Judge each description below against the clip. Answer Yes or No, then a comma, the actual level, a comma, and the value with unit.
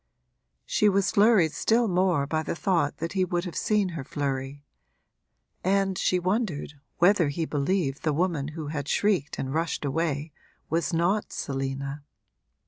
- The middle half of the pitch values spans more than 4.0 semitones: Yes, average, 4.7 semitones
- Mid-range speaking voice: Yes, medium, 165 Hz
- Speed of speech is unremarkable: Yes, average, 150 wpm